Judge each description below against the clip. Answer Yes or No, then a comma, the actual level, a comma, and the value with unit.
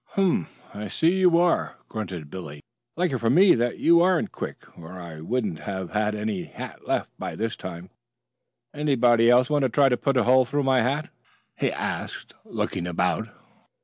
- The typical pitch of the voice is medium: No, low, 120 Hz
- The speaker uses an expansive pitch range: Yes, wide, 7.5 semitones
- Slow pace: No, average, 180 wpm